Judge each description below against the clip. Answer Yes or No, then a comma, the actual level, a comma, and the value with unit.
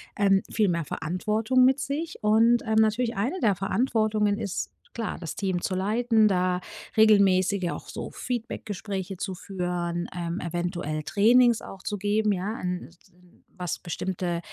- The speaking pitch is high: Yes, high, 200 Hz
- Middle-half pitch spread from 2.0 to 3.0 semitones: No, average, 3.5 semitones